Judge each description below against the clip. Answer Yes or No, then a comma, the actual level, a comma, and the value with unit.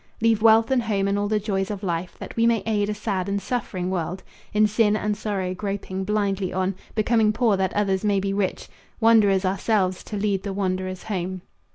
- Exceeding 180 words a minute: Yes, fast, 205 wpm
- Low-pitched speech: No, high, 200 Hz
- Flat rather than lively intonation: Yes, narrow, 2.1 semitones